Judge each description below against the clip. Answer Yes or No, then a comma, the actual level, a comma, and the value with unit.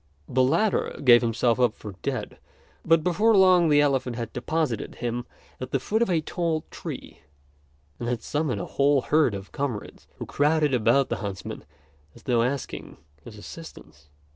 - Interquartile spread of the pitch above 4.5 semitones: Yes, average, 5.0 semitones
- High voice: No, low, 135 Hz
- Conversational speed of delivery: Yes, average, 165 wpm